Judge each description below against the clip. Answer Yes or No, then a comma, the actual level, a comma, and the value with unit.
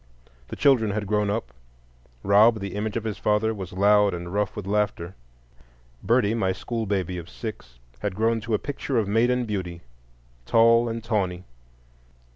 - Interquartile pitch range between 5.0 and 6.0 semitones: No, average, 2.8 semitones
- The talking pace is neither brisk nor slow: Yes, average, 165 wpm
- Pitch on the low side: Yes, low, 105 Hz